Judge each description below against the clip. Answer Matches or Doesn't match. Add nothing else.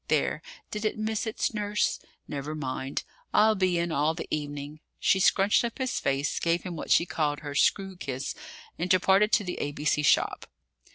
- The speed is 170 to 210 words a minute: Matches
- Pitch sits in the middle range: Matches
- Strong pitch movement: Matches